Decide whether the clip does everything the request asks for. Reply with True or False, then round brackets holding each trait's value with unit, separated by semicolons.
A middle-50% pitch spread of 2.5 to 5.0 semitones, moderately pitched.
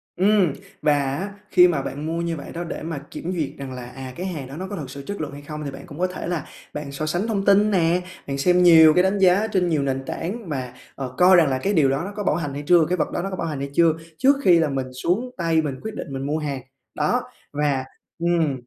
True (4.5 semitones; 160 Hz)